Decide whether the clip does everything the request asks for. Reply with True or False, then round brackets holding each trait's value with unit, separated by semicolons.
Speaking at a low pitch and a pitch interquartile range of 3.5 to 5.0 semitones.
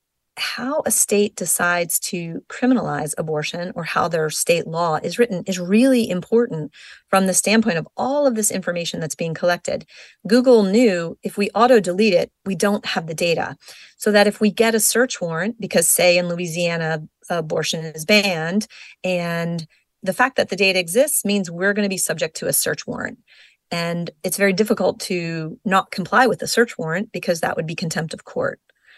False (190 Hz; 4.7 semitones)